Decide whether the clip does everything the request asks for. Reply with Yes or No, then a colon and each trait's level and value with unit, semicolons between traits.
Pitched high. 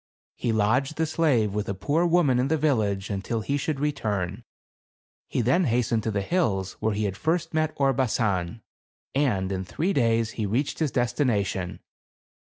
No: low, 120 Hz